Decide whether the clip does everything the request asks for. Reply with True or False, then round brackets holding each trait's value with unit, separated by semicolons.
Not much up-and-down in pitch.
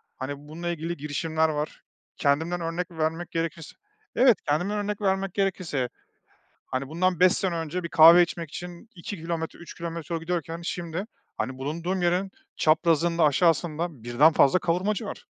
True (2.2 semitones)